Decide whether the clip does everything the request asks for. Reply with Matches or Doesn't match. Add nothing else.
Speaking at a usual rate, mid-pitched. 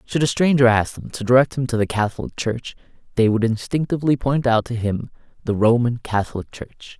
Doesn't match